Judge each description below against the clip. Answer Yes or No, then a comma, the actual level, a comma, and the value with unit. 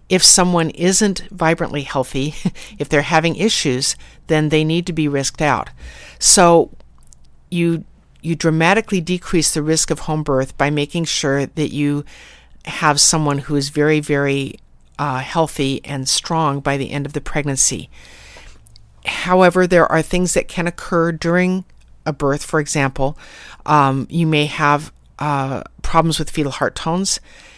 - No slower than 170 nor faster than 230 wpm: No, average, 150 wpm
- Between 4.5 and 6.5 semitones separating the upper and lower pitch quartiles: No, average, 3.4 semitones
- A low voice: No, medium, 150 Hz